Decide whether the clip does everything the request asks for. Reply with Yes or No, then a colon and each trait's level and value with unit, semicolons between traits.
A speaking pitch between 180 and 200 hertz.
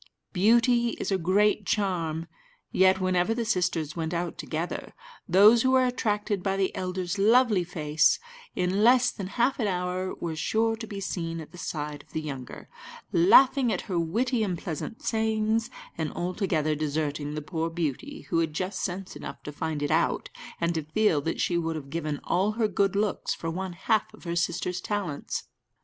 Yes: medium, 185 Hz